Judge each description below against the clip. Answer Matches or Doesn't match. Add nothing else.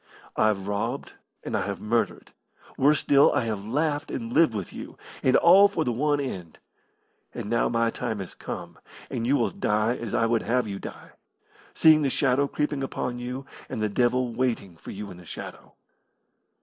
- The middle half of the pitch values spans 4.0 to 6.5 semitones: Matches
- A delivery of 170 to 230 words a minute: Matches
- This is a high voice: Doesn't match